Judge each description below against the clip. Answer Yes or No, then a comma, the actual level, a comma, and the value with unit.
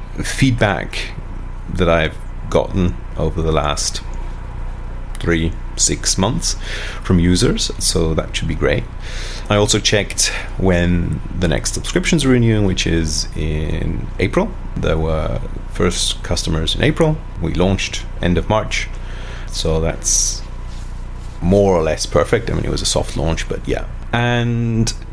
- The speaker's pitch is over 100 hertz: No, very low, 90 Hz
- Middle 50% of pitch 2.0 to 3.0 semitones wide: No, average, 3.7 semitones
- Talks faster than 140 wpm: No, slow, 135 wpm